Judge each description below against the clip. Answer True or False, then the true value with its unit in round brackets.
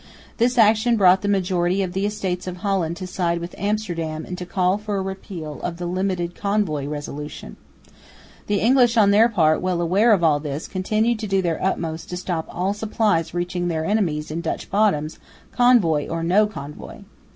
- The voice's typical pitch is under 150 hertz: False (185 Hz)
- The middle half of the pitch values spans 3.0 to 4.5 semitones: True (3.7 semitones)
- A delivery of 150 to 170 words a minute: False (185 wpm)